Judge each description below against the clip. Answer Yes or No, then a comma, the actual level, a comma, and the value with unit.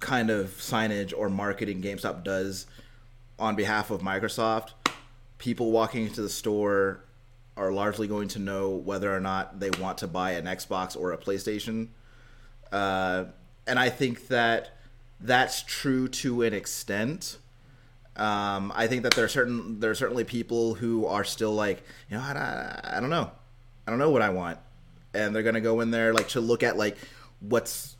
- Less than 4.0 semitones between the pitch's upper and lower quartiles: Yes, average, 3.2 semitones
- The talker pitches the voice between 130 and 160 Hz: No, low, 110 Hz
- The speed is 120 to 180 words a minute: Yes, average, 175 wpm